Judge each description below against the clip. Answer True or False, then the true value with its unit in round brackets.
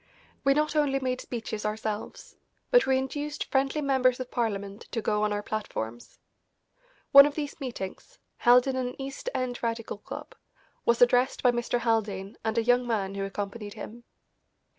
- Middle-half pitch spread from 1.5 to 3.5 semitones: False (4.0 semitones)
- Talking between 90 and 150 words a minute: False (165 wpm)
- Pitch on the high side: True (240 Hz)